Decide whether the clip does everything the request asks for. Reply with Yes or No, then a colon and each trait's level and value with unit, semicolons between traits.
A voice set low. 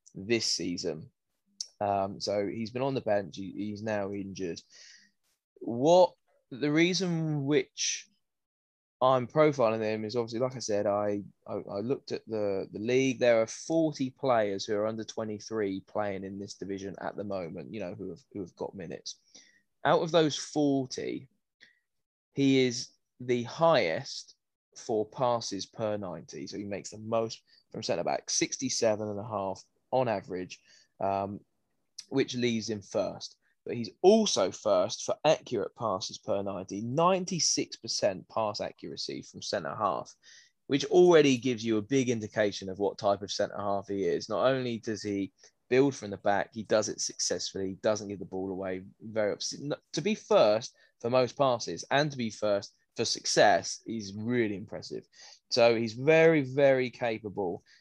Yes: low, 110 Hz